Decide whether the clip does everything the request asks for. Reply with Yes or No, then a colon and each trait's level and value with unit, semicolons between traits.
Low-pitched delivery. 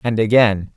Yes: low, 110 Hz